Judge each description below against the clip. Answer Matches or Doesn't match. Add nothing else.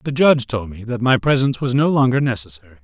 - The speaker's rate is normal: Doesn't match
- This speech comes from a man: Matches